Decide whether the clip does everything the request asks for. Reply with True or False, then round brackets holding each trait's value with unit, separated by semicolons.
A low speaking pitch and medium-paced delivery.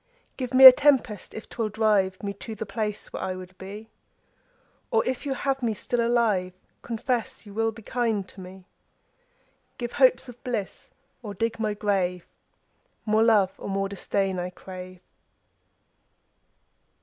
False (215 Hz; 160 wpm)